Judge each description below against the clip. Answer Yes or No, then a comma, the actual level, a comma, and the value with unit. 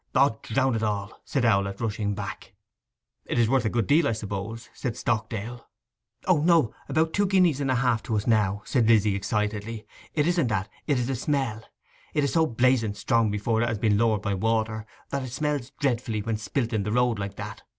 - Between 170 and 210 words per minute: Yes, average, 200 wpm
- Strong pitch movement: No, average, 3.8 semitones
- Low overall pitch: Yes, low, 115 Hz